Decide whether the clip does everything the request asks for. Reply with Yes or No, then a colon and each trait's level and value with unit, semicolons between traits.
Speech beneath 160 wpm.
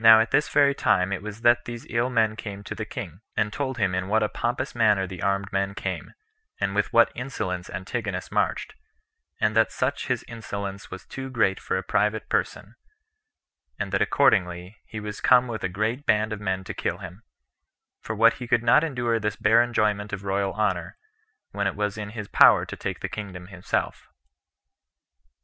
No: average, 195 wpm